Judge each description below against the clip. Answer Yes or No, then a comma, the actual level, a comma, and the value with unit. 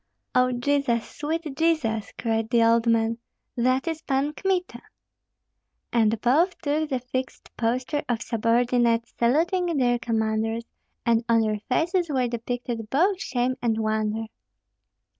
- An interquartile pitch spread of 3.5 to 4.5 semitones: Yes, average, 4.2 semitones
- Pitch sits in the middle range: No, high, 245 Hz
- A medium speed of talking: No, slow, 130 wpm